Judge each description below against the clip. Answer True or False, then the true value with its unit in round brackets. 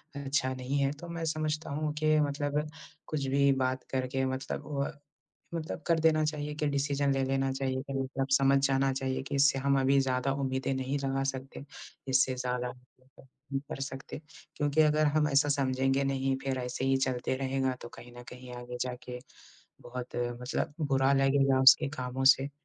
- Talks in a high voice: False (135 Hz)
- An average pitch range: False (1.4 semitones)